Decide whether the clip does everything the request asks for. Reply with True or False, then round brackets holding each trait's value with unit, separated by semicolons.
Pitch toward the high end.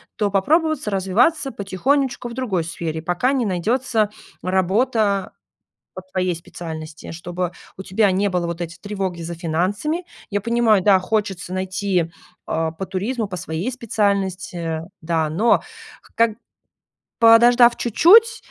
True (195 Hz)